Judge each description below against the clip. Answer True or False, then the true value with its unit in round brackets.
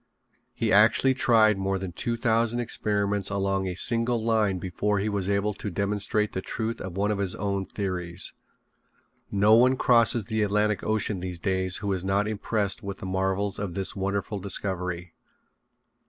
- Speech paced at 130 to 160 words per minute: False (170 wpm)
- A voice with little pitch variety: True (2.1 semitones)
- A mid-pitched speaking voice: False (100 Hz)